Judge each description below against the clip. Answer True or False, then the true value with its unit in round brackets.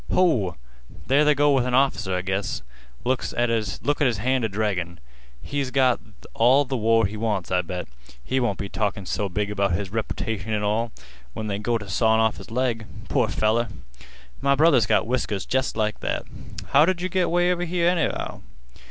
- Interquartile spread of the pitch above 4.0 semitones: True (4.6 semitones)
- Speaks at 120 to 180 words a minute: False (190 wpm)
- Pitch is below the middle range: True (115 Hz)